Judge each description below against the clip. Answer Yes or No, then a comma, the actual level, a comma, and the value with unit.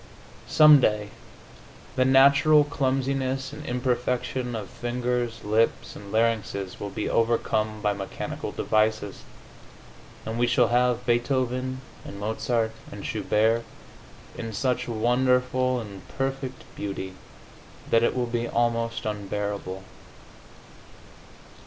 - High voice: No, low, 120 Hz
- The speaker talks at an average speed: No, slow, 110 wpm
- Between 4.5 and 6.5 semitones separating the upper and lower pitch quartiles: No, average, 2.9 semitones